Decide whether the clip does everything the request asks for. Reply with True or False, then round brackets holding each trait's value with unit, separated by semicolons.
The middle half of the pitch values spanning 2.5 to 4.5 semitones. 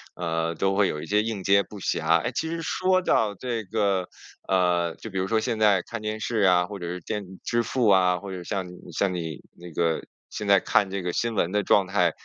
True (3.2 semitones)